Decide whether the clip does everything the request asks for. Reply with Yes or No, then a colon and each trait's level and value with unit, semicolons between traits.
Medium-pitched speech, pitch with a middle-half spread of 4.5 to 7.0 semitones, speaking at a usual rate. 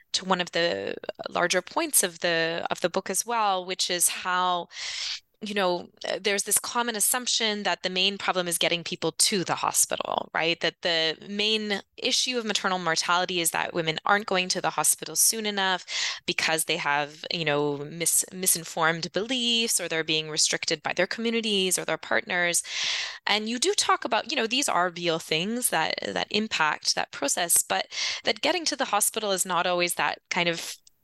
No: medium, 180 Hz; average, 4.0 semitones; average, 185 wpm